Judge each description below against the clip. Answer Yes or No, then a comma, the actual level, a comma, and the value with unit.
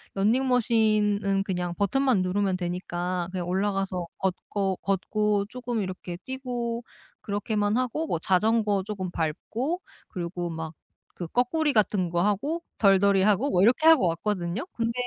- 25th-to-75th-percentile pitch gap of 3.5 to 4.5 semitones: Yes, average, 4.2 semitones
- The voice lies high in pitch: Yes, high, 200 Hz